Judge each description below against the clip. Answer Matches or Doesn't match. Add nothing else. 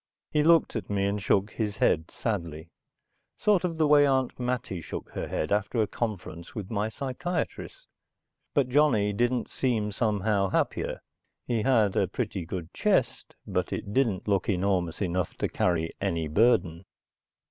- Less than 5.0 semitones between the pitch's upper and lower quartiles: Doesn't match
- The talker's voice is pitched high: Doesn't match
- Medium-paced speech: Matches